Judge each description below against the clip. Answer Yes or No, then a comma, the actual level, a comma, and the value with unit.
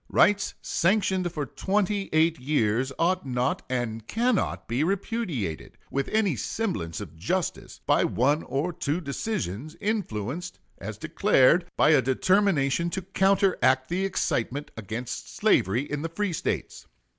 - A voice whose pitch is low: No, medium, 155 Hz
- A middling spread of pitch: No, wide, 7.1 semitones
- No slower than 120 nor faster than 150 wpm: Yes, slow, 135 wpm